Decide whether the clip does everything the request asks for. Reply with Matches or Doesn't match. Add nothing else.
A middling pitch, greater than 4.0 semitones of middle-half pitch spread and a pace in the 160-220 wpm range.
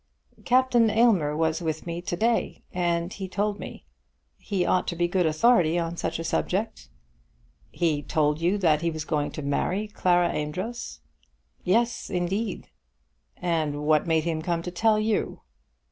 Matches